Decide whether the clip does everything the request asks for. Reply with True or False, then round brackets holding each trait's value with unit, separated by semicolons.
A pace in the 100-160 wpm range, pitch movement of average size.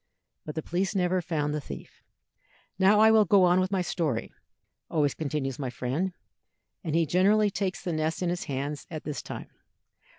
False (185 wpm; 4.1 semitones)